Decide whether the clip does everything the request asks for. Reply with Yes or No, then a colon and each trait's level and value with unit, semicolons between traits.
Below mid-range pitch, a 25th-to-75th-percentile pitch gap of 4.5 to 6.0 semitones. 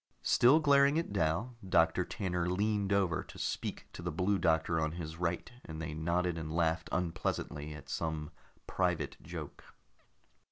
No: very low, 85 Hz; average, 3.6 semitones